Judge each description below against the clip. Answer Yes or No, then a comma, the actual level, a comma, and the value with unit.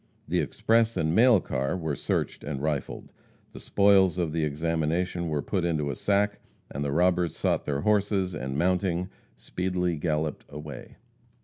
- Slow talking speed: No, average, 155 wpm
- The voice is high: No, very low, 85 Hz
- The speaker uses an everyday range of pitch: Yes, average, 3.8 semitones